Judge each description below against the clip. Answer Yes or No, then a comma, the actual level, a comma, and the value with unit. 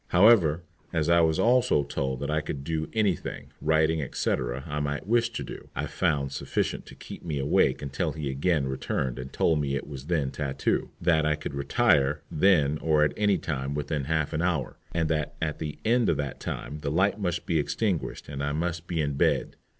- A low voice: Yes, very low, 75 Hz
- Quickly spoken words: Yes, fast, 210 wpm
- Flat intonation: No, average, 3.2 semitones